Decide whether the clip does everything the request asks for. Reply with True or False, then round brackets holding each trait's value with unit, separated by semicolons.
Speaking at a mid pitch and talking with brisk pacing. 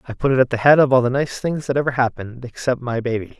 False (125 Hz; 300 wpm)